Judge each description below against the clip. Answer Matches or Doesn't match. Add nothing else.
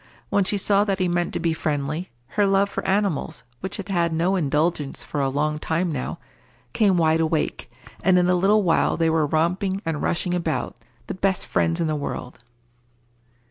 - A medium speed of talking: Matches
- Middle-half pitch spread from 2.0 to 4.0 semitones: Matches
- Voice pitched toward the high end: Doesn't match